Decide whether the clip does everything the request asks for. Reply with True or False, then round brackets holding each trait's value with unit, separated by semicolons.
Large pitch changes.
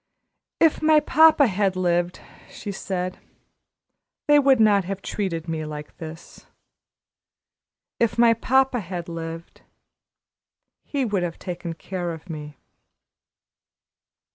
True (5.7 semitones)